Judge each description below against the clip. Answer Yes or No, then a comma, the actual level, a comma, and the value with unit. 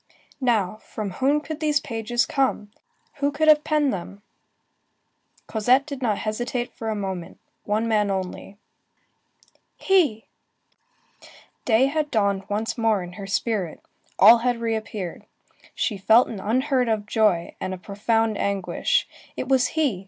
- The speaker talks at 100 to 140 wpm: Yes, slow, 135 wpm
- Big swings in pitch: No, average, 4.4 semitones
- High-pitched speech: Yes, high, 225 Hz